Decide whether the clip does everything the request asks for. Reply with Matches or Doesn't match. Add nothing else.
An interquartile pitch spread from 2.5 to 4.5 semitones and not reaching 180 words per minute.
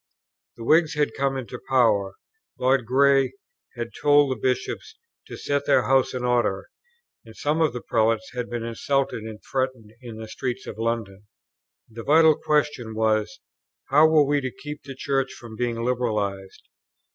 Matches